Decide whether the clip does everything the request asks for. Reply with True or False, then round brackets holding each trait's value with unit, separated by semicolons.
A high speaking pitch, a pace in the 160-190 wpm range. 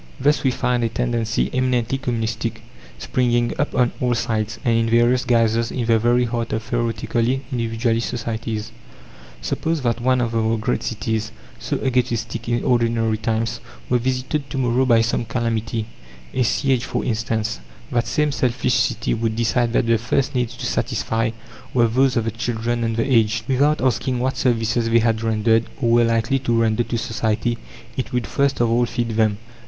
False (115 Hz; 180 wpm)